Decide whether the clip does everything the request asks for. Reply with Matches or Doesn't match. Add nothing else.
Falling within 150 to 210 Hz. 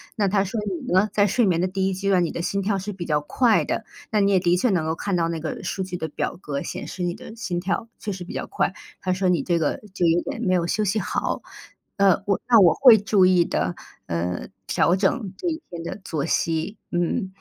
Matches